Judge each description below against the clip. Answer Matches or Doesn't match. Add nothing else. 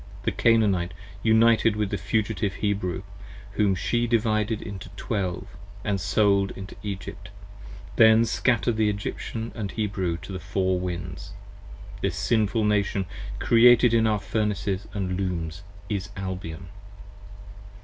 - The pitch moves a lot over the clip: Doesn't match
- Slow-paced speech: Matches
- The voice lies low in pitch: Matches